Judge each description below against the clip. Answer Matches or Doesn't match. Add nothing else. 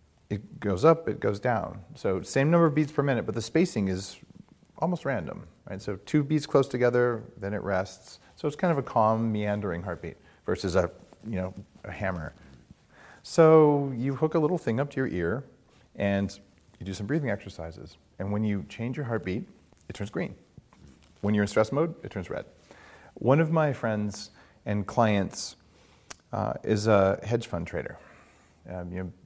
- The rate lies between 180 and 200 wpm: Matches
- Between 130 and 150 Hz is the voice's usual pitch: Doesn't match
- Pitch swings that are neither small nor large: Doesn't match